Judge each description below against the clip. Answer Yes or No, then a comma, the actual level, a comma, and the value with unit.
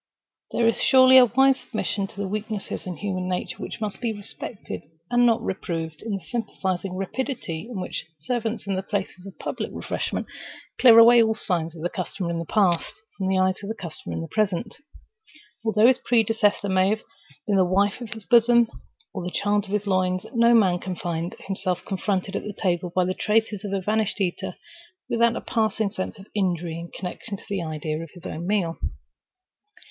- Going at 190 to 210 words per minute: Yes, average, 195 wpm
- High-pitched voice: Yes, high, 195 Hz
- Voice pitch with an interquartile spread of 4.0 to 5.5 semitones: No, average, 3.5 semitones